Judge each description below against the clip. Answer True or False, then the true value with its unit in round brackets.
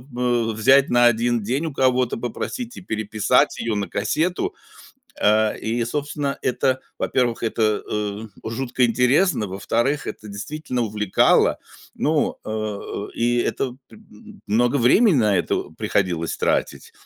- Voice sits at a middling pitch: False (120 Hz)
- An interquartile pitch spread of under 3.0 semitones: False (3.6 semitones)